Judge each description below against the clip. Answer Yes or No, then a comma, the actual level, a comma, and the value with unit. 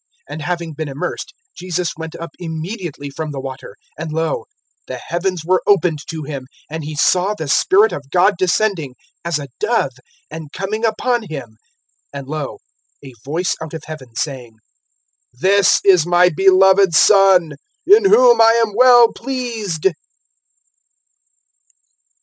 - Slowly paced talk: No, average, 145 wpm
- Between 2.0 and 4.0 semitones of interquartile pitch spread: No, average, 4.8 semitones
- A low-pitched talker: No, medium, 175 Hz